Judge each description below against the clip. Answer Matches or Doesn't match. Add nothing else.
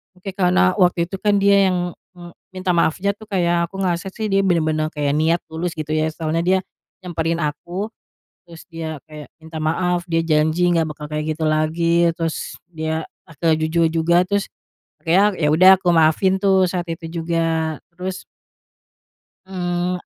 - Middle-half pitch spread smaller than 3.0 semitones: Matches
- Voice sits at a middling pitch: Matches